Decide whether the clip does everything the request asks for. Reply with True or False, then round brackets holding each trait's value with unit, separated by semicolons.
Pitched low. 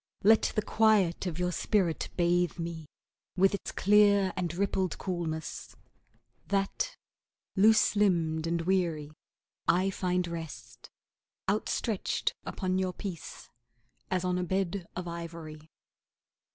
False (180 Hz)